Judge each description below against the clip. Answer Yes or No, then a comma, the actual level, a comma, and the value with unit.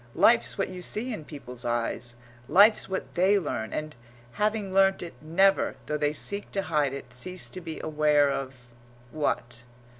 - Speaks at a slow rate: No, average, 170 wpm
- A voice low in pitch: No, medium, 155 Hz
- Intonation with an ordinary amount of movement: No, wide, 5.9 semitones